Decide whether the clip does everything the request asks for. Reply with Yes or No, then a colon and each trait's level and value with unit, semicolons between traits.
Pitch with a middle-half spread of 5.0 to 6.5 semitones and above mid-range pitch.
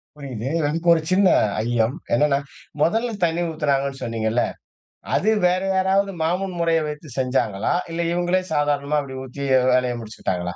No: wide, 5.6 semitones; medium, 145 Hz